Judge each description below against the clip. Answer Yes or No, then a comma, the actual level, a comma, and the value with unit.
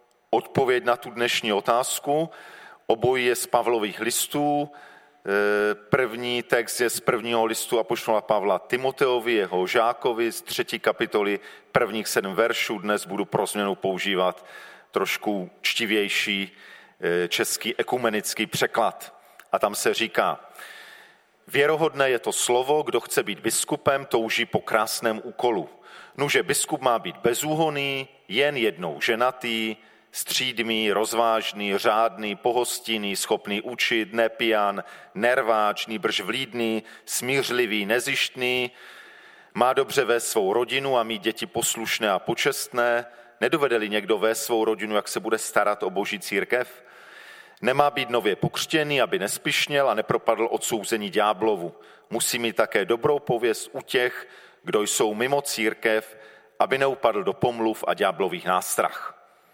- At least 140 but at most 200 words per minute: No, average, 125 wpm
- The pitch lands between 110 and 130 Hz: Yes, low, 115 Hz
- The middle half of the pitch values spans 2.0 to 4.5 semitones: Yes, narrow, 2.5 semitones